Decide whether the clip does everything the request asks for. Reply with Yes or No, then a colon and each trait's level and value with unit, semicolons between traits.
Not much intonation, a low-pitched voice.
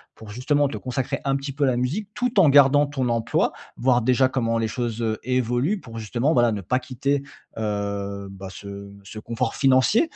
No: average, 3.7 semitones; low, 125 Hz